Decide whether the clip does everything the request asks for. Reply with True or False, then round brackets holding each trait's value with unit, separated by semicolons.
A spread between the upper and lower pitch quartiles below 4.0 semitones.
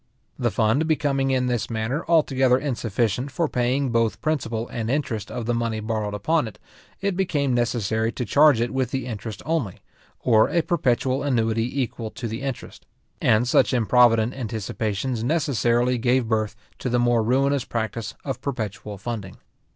True (3.3 semitones)